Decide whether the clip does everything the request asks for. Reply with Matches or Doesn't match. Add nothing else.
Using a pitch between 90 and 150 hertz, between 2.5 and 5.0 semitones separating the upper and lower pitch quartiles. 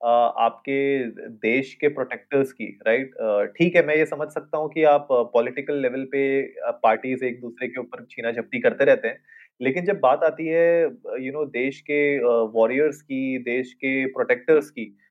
Matches